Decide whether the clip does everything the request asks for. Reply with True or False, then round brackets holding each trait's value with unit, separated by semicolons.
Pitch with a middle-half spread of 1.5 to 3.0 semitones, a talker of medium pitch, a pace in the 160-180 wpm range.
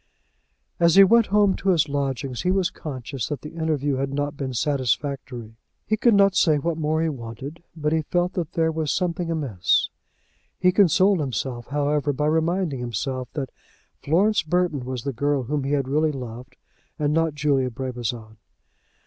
False (4.1 semitones; 145 Hz; 175 wpm)